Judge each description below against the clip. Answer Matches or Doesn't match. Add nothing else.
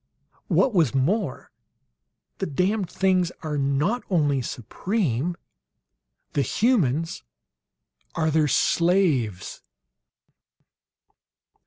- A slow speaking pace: Matches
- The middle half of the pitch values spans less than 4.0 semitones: Doesn't match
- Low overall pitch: Doesn't match